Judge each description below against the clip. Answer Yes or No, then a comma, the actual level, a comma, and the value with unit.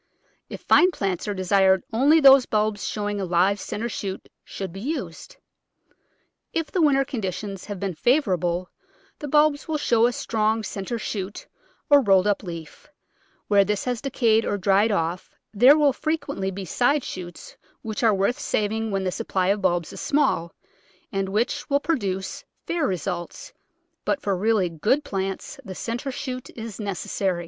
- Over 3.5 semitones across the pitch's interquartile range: Yes, average, 5.1 semitones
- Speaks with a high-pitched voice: Yes, high, 210 Hz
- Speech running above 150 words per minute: Yes, average, 165 wpm